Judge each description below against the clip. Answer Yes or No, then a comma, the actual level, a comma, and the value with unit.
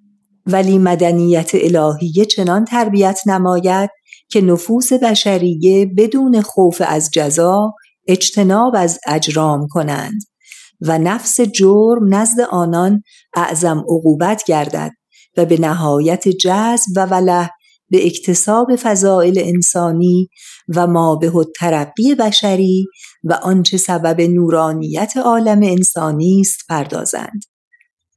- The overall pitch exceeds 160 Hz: Yes, medium, 185 Hz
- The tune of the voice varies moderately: Yes, average, 3.6 semitones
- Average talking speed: No, slow, 100 wpm